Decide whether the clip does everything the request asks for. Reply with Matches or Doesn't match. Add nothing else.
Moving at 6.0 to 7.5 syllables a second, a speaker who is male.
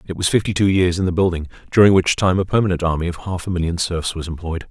Matches